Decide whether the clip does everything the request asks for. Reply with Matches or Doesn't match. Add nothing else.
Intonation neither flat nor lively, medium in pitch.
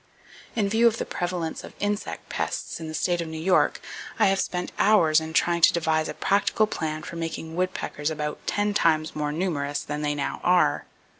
Matches